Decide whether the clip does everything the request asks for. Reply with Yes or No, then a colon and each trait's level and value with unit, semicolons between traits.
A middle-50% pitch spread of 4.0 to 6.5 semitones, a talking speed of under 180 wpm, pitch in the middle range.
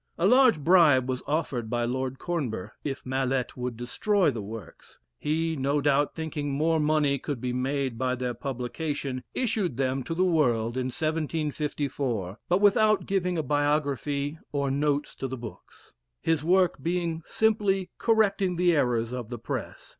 Yes: average, 4.5 semitones; average, 160 wpm; medium, 145 Hz